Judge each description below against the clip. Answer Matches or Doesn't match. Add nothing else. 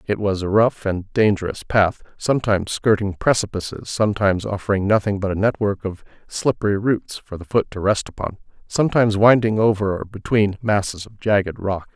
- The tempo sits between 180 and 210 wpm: Doesn't match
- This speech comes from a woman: Doesn't match